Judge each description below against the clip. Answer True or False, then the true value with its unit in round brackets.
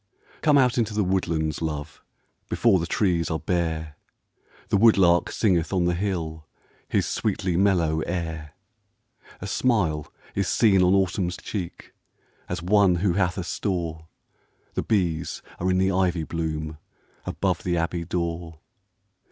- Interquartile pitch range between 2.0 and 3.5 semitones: True (2.9 semitones)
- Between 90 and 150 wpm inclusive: True (140 wpm)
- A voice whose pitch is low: True (90 Hz)